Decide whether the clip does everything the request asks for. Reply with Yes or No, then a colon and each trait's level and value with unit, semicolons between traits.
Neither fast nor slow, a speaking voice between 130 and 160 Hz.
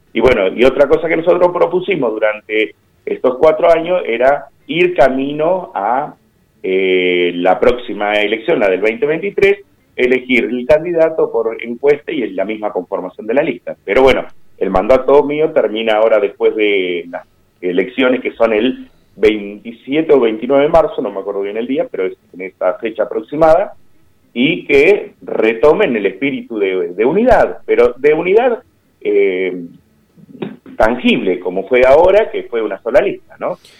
Yes: average, 160 wpm; medium, 140 Hz